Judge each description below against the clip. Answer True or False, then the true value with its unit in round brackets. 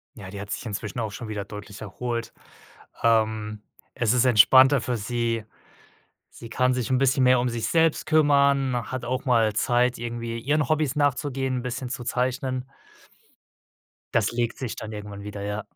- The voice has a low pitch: True (120 Hz)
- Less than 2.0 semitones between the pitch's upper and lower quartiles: False (2.9 semitones)